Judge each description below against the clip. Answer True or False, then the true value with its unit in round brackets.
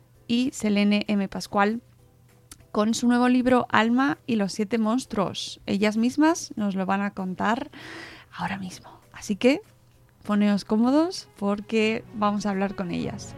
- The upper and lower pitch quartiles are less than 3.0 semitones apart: False (3.3 semitones)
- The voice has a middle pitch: False (215 Hz)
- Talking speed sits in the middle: True (145 wpm)